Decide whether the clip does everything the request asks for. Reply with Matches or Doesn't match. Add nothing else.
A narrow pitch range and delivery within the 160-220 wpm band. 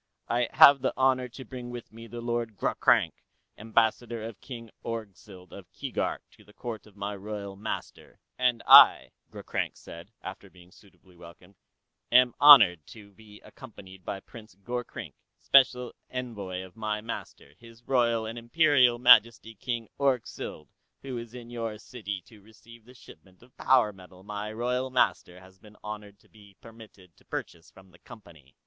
Doesn't match